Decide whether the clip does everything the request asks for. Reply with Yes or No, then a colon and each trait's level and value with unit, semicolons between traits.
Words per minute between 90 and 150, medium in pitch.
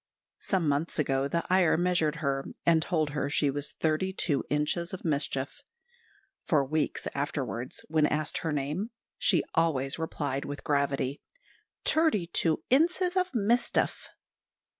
Yes: average, 140 wpm; medium, 155 Hz